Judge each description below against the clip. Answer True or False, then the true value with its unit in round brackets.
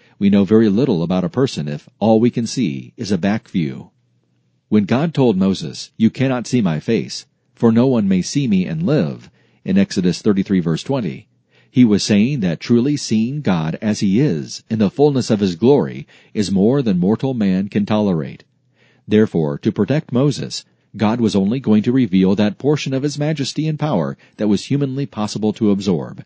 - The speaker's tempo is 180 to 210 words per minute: True (190 wpm)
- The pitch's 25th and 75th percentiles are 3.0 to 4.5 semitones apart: False (5.5 semitones)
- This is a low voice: True (110 Hz)